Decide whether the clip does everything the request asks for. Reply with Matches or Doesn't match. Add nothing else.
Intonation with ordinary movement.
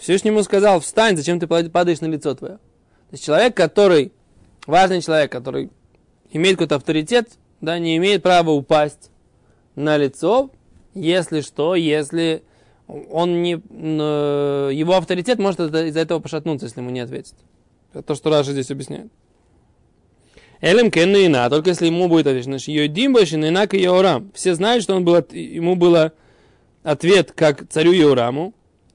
Matches